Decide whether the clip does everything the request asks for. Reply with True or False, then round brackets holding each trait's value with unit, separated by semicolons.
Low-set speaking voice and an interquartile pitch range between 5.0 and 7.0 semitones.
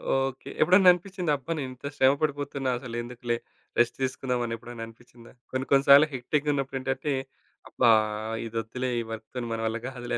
False (130 Hz; 2.7 semitones)